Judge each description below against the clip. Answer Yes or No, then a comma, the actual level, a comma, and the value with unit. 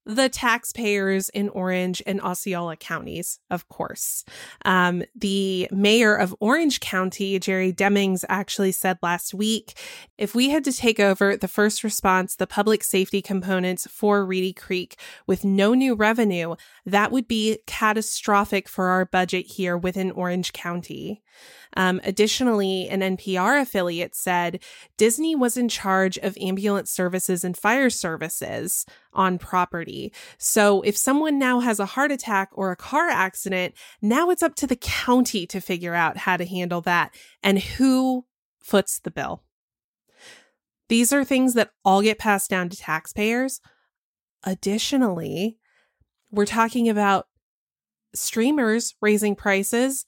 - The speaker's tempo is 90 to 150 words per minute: Yes, average, 140 wpm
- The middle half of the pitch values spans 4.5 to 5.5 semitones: No, average, 3.2 semitones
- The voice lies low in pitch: No, high, 200 Hz